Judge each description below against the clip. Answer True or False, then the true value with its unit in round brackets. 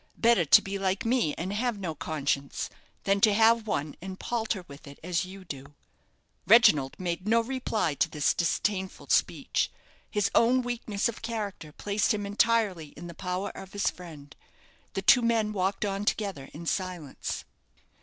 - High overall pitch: True (195 Hz)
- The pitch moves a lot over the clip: False (4.7 semitones)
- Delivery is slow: False (165 wpm)